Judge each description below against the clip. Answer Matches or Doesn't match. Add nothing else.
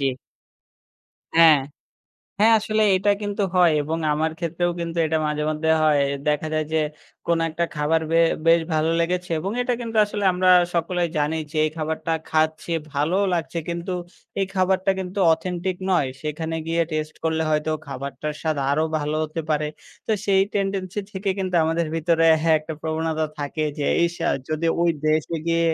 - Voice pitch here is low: Doesn't match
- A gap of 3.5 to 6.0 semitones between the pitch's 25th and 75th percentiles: Doesn't match